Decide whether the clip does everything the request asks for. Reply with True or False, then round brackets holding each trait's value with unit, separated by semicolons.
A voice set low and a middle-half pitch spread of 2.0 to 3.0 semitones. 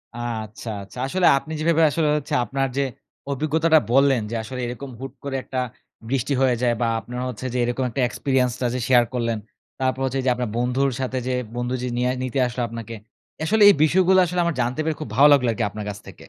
True (130 Hz; 2.7 semitones)